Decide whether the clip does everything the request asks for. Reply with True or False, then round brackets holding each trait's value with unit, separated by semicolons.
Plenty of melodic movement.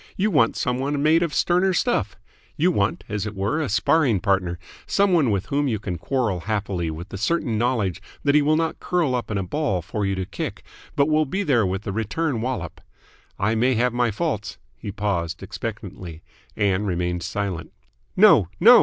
True (7.3 semitones)